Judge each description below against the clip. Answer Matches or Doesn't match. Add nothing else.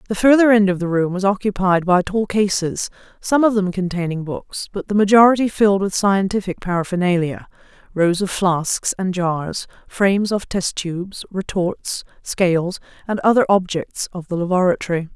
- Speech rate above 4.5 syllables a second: Matches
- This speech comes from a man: Doesn't match